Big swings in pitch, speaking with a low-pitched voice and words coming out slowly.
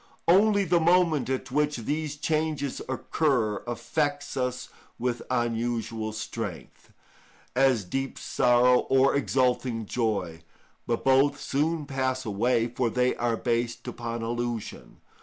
No: average, 3.5 semitones; low, 125 Hz; slow, 120 wpm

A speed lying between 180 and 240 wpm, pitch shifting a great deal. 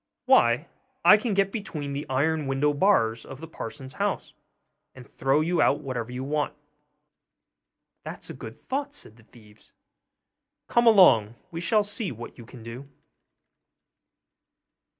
No: average, 145 wpm; wide, 7.3 semitones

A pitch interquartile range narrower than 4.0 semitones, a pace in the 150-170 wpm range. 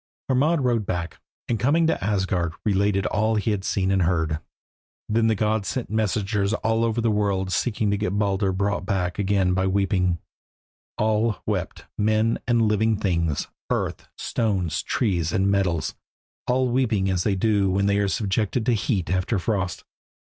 Yes: average, 2.7 semitones; average, 165 wpm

